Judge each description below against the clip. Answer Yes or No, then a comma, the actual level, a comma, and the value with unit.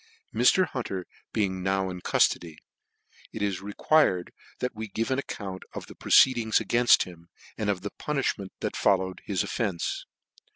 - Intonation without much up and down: No, average, 4.1 semitones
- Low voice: Yes, low, 100 Hz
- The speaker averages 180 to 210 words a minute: No, average, 160 wpm